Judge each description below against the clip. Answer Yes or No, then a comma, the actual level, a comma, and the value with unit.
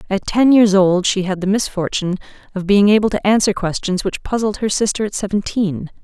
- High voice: Yes, high, 200 Hz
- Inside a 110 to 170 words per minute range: No, average, 200 wpm